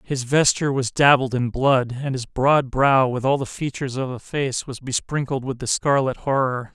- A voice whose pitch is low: Yes, low, 130 Hz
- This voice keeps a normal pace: Yes, average, 195 wpm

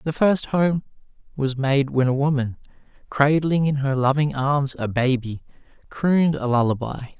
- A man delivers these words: Yes, male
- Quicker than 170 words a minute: No, average, 150 wpm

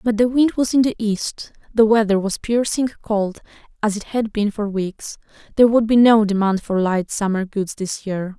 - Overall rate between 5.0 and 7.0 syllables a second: No, 4.8 syllables/s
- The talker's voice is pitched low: No, high, 215 Hz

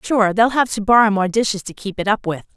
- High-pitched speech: Yes, high, 210 Hz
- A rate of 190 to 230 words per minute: No, fast, 280 wpm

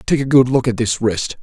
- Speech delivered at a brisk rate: Yes, fast, 295 wpm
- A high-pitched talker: No, low, 125 Hz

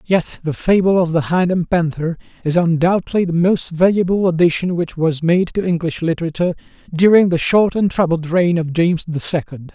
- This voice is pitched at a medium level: Yes, medium, 170 Hz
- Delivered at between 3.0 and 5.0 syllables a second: No, 5.4 syllables/s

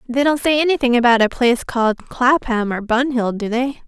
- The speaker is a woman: Yes, female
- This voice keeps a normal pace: No, fast, 215 wpm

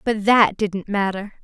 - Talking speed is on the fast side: No, average, 165 wpm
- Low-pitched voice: No, high, 205 Hz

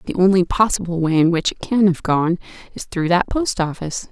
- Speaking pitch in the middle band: Yes, medium, 180 Hz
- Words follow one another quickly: Yes, fast, 220 wpm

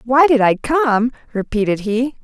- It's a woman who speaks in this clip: Yes, female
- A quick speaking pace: No, average, 160 wpm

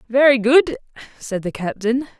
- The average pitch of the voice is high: Yes, high, 235 Hz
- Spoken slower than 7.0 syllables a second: Yes, 4.6 syllables/s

